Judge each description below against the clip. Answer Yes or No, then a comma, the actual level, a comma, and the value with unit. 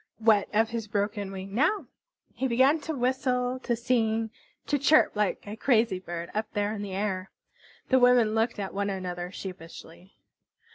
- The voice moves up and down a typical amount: Yes, average, 4.1 semitones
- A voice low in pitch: No, high, 220 Hz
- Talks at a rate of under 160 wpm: No, average, 165 wpm